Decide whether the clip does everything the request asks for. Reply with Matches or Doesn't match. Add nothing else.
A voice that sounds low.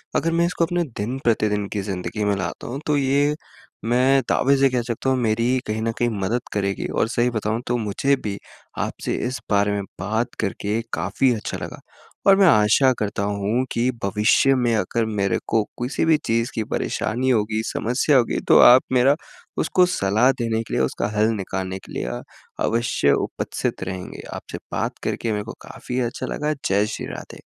Matches